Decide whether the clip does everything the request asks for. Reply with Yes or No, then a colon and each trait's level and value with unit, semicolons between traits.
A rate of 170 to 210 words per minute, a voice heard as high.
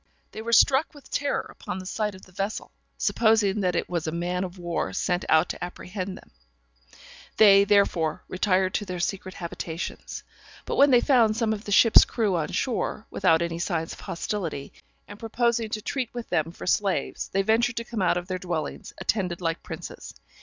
Yes: average, 195 wpm; high, 195 Hz